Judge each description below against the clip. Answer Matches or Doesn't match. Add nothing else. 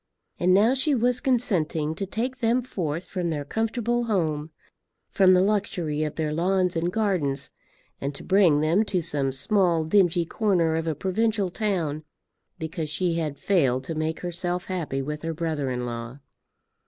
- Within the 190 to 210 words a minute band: Doesn't match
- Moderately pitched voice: Matches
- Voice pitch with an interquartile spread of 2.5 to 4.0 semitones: Doesn't match